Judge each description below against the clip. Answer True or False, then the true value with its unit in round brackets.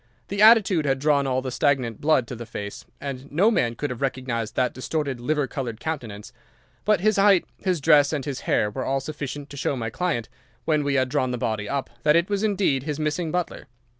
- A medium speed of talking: False (220 wpm)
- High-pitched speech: False (140 Hz)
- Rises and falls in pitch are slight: False (3.9 semitones)